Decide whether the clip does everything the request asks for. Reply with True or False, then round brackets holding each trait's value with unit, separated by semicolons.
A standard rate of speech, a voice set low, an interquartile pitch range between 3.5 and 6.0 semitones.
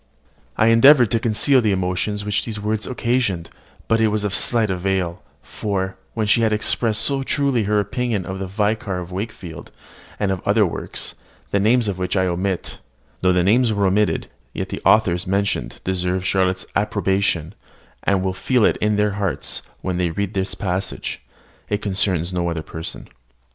False (175 wpm; 100 Hz; 2.8 semitones)